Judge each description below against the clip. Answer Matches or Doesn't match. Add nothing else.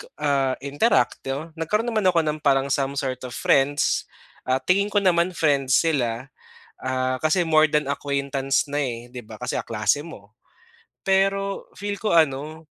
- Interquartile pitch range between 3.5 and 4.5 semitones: Matches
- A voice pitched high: Doesn't match